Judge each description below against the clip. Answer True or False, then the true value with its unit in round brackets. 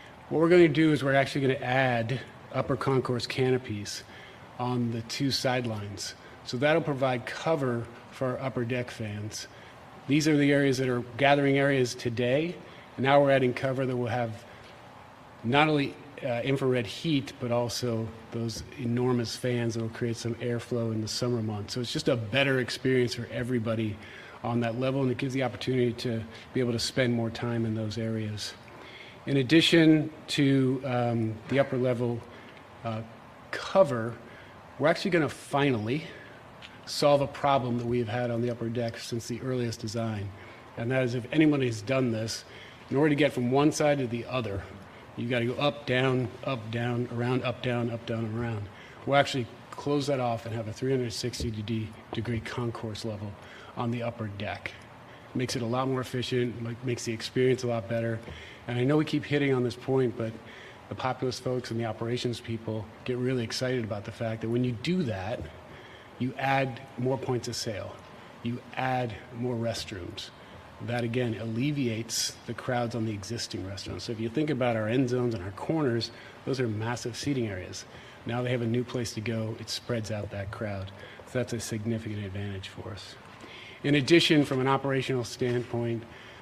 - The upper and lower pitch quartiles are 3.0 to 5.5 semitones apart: False (2.4 semitones)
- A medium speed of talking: True (185 wpm)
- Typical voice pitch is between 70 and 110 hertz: False (120 Hz)